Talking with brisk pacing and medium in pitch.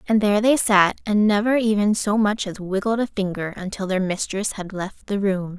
No: fast, 215 wpm; high, 200 Hz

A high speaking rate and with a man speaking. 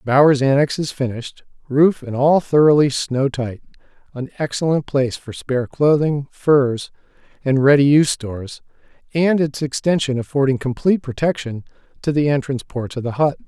No: average, 150 wpm; male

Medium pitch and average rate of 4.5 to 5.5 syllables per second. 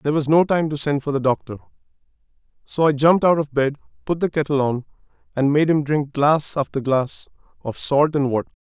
No: medium, 145 Hz; 5.8 syllables/s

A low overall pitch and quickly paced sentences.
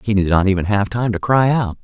Yes: low, 105 Hz; fast, 295 wpm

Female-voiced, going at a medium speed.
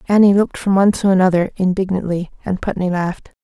Yes: female; average, 175 wpm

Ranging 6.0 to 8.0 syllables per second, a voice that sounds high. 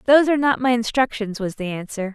Yes: 6.5 syllables/s; high, 235 Hz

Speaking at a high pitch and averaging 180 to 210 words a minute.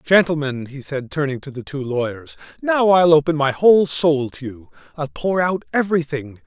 No: medium, 150 Hz; average, 185 wpm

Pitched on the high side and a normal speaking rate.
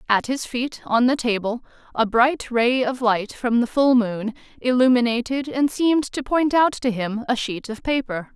Yes: high, 245 Hz; average, 195 wpm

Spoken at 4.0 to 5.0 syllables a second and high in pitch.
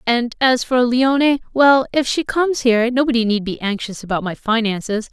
No: 5.3 syllables/s; high, 240 Hz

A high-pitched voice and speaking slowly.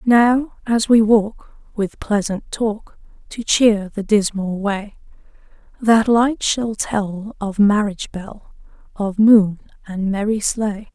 Yes: high, 210 Hz; slow, 130 wpm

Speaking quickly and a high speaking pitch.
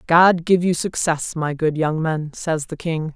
No: fast, 210 wpm; medium, 160 Hz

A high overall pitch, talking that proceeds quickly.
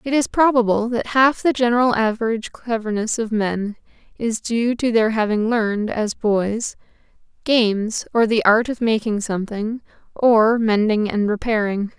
No: high, 225 Hz; average, 150 wpm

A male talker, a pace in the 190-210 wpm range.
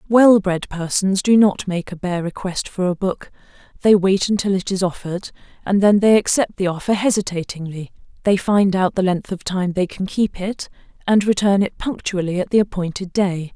No: female; average, 195 wpm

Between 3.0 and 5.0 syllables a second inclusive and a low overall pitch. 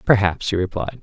No: 5.6 syllables/s; low, 100 Hz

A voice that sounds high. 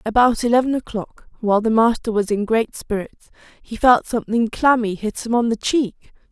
Yes: high, 225 Hz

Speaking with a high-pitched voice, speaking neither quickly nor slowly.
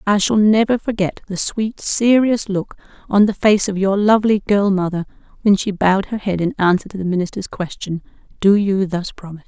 Yes: high, 200 Hz; average, 195 wpm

